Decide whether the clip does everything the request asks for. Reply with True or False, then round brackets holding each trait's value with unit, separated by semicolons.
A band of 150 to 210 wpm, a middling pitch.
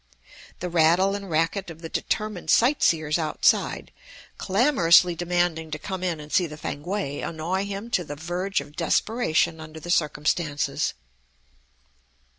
False (140 wpm; 170 Hz)